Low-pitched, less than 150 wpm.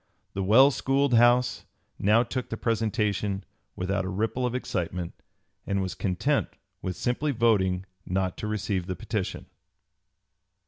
Yes: low, 105 Hz; slow, 135 wpm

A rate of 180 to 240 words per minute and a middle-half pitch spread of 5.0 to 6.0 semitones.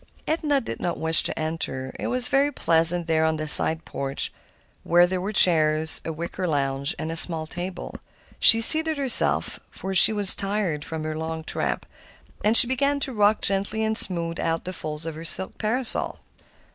Yes: average, 185 wpm; wide, 5.4 semitones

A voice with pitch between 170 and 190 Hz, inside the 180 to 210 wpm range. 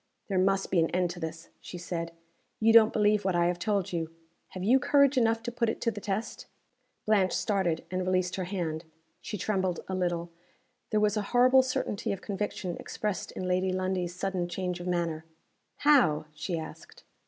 Yes: medium, 185 Hz; average, 190 wpm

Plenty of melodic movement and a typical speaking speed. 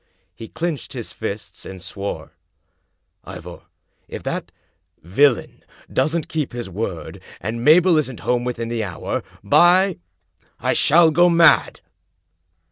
No: wide, 6.8 semitones; slow, 125 wpm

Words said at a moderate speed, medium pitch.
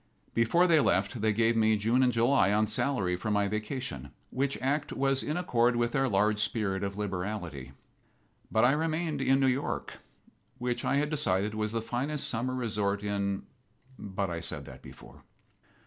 No: average, 175 wpm; low, 115 Hz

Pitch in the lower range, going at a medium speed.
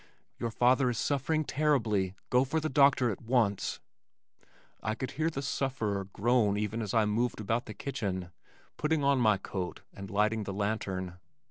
Yes: low, 115 Hz; average, 165 wpm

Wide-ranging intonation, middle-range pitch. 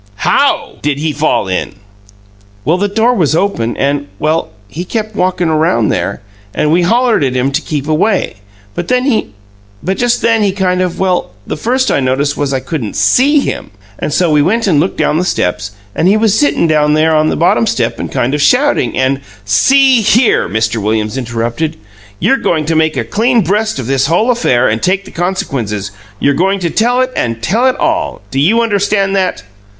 Yes: wide, 7.5 semitones; medium, 160 Hz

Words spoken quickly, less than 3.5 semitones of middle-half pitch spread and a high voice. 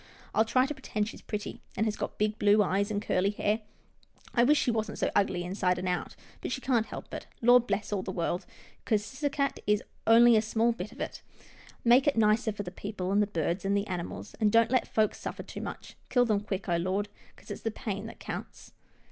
Yes: fast, 230 wpm; average, 2.7 semitones; high, 210 Hz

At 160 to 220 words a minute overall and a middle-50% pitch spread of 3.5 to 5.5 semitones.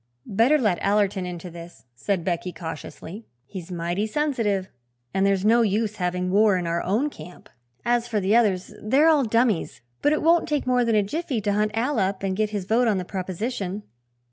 Yes: average, 195 wpm; average, 4.1 semitones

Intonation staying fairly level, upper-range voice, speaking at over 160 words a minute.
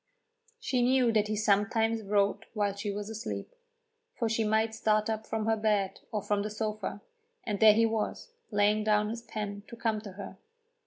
Yes: narrow, 1.3 semitones; high, 215 Hz; average, 190 wpm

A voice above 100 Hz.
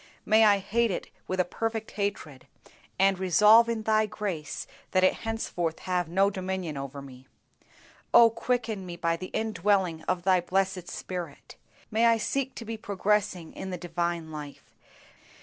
Yes: high, 190 Hz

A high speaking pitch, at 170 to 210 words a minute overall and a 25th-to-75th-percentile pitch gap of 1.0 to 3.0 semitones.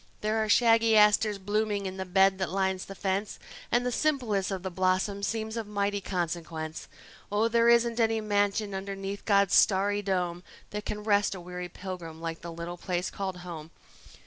Yes: high, 200 Hz; average, 180 wpm; narrow, 2.5 semitones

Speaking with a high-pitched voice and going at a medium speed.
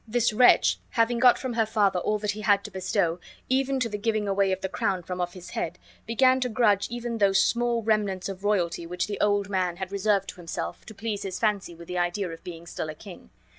No: high, 200 Hz; fast, 240 wpm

